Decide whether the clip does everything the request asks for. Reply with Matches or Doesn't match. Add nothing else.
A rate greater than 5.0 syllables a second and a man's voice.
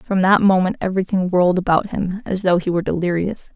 Doesn't match